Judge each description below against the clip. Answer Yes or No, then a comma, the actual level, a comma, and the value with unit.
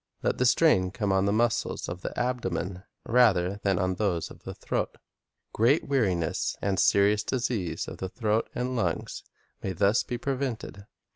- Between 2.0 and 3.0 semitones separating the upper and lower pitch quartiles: No, average, 4.6 semitones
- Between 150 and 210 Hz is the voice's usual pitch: No, low, 105 Hz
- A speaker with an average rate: Yes, average, 170 wpm